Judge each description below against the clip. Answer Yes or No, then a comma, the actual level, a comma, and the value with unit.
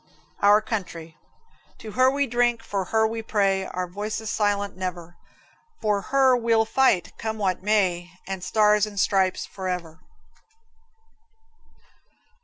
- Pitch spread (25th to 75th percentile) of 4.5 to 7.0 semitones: No, average, 3.1 semitones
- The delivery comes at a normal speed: No, slow, 125 wpm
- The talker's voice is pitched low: No, high, 205 Hz